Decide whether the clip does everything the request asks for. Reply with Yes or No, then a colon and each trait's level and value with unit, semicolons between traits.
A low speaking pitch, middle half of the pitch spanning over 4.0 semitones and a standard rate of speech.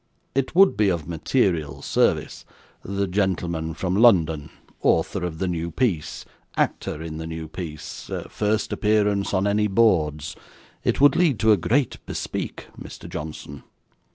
Yes: very low, 90 Hz; average, 4.7 semitones; average, 145 wpm